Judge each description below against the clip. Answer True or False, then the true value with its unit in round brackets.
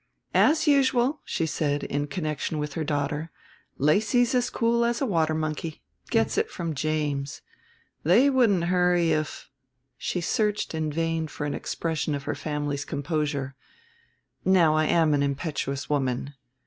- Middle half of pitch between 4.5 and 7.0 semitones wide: False (4.1 semitones)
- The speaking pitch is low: False (155 Hz)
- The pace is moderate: True (150 wpm)